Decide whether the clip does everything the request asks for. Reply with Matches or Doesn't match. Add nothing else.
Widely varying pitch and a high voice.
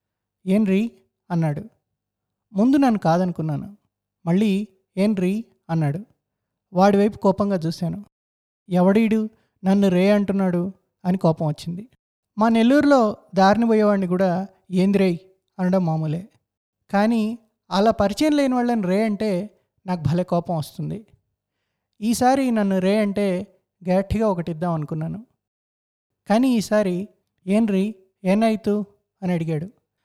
Doesn't match